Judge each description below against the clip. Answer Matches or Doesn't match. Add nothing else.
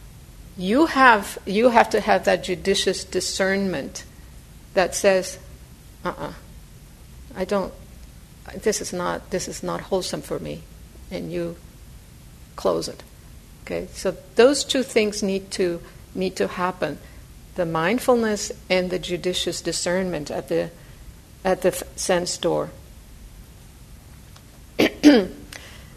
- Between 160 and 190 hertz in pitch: Matches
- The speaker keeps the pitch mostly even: Matches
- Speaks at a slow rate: Matches